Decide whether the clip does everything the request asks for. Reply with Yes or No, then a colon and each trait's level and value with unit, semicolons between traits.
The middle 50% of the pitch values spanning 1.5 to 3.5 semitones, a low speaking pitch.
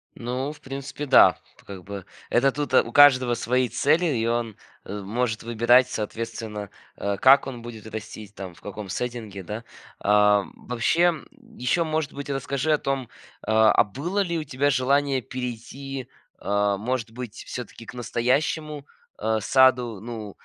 No: average, 4.0 semitones; low, 120 Hz